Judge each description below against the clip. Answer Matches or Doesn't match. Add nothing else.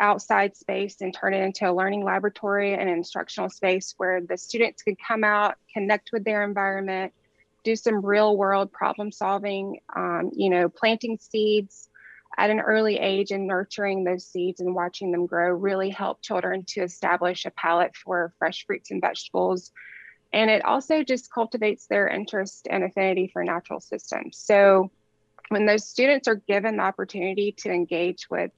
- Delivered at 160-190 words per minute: Matches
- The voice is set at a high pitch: Matches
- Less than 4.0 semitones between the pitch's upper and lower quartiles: Matches